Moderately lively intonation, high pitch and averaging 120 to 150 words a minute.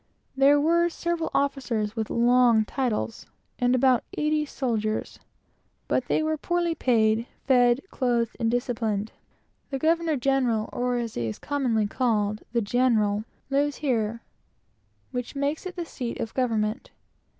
Yes: average, 4.1 semitones; high, 245 Hz; average, 140 wpm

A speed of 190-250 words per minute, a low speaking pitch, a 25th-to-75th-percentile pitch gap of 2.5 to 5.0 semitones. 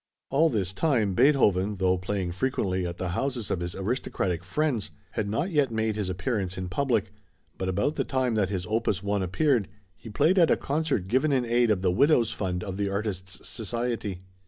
No: average, 195 wpm; low, 105 Hz; wide, 5.5 semitones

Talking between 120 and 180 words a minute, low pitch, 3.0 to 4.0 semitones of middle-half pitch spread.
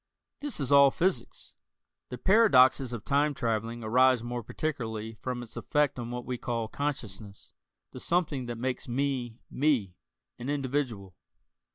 Yes: average, 145 wpm; low, 125 Hz; average, 3.5 semitones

